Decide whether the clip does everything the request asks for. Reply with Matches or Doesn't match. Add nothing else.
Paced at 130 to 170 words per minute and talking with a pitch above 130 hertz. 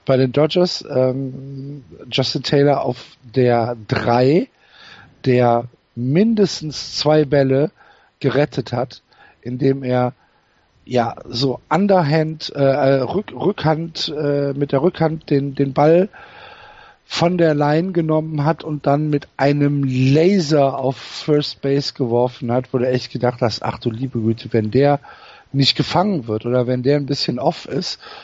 Matches